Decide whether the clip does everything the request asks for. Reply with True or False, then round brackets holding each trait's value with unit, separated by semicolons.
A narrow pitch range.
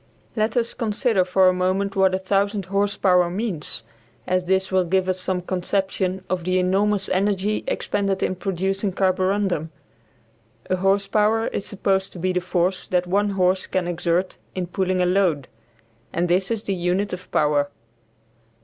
True (1.6 semitones)